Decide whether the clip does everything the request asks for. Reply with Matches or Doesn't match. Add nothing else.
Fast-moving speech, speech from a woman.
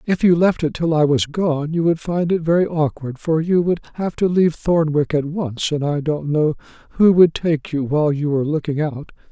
Doesn't match